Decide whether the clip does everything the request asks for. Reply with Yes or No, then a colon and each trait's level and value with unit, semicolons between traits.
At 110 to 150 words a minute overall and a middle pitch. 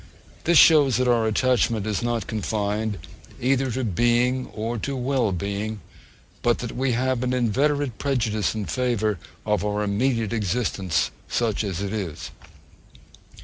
No: average, 145 wpm; low, 115 Hz